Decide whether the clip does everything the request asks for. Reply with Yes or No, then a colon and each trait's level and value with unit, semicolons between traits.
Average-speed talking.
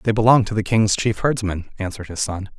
No: fast, 230 wpm